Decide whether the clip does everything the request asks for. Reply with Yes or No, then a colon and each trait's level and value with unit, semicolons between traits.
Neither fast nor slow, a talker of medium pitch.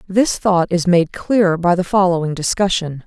Yes: average, 175 wpm; medium, 180 Hz